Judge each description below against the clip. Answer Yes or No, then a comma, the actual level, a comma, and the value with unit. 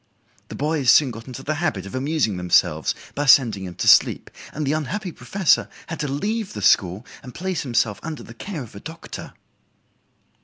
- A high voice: No, medium, 140 Hz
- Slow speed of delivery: No, average, 190 wpm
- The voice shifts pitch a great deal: Yes, wide, 6.1 semitones